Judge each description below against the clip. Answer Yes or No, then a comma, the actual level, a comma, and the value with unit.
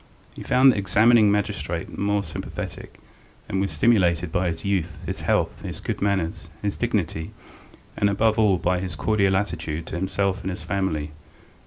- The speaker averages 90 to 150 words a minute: No, average, 160 wpm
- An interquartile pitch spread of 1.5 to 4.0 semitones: Yes, average, 2.9 semitones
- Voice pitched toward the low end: Yes, very low, 95 Hz